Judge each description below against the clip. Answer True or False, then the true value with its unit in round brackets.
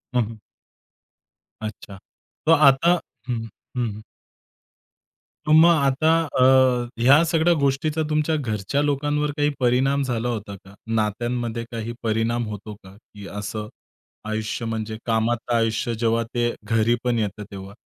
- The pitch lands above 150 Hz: False (115 Hz)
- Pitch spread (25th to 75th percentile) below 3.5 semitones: False (4.2 semitones)